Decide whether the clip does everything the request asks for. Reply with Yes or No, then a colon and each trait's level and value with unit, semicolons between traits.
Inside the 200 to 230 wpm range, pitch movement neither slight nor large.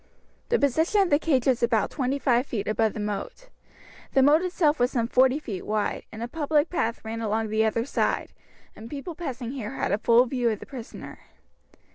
Yes: fast, 205 wpm; average, 4.5 semitones